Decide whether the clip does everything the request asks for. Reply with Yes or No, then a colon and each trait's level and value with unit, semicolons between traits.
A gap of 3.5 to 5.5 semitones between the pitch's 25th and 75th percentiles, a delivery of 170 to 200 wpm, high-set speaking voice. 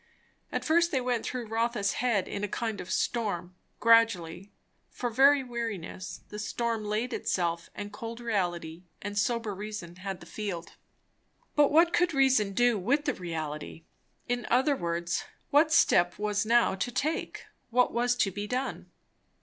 No: average, 4.5 semitones; average, 160 wpm; high, 220 Hz